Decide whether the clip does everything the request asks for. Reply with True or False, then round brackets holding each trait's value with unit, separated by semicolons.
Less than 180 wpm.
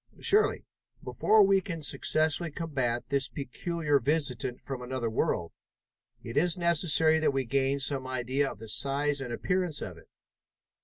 True (150 wpm)